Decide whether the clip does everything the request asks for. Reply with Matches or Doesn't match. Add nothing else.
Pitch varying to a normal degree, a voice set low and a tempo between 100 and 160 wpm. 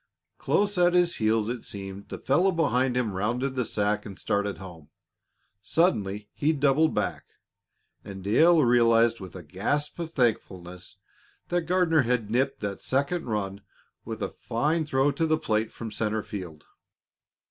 Doesn't match